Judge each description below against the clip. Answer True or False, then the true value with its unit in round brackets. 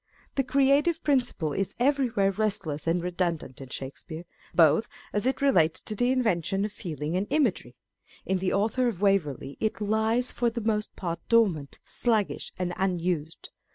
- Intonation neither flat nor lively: False (5.8 semitones)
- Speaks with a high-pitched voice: True (195 Hz)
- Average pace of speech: True (155 wpm)